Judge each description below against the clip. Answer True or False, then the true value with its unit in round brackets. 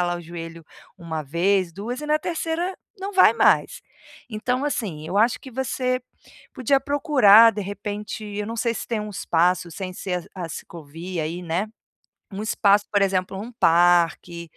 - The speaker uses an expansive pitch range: True (5.7 semitones)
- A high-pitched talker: True (200 Hz)